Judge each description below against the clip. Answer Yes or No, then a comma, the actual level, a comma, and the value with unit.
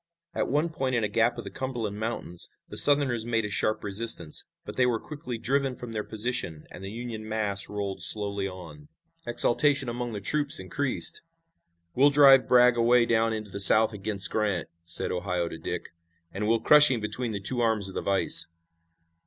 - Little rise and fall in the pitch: No, average, 3.7 semitones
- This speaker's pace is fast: No, average, 190 wpm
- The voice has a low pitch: Yes, low, 115 Hz